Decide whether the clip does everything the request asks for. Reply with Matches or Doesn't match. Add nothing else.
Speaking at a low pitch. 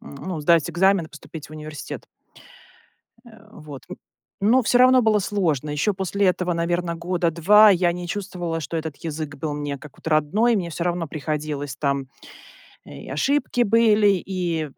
Doesn't match